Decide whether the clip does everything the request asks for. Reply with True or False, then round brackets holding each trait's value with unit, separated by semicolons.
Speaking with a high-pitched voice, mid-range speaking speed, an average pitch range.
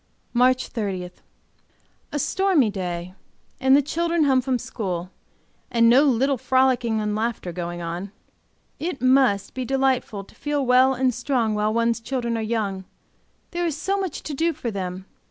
True (245 Hz; 160 wpm; 4.5 semitones)